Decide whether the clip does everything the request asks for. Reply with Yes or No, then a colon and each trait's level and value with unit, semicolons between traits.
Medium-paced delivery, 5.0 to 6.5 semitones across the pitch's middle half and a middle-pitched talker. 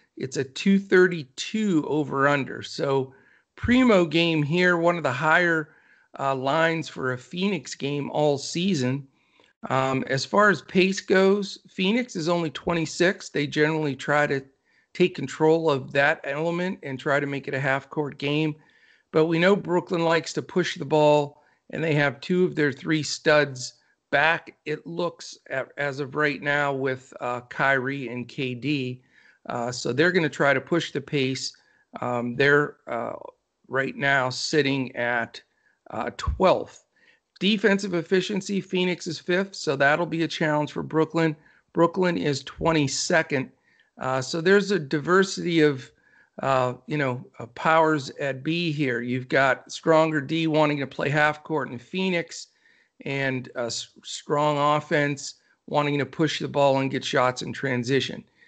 No: average, 155 wpm; average, 3.7 semitones; medium, 150 Hz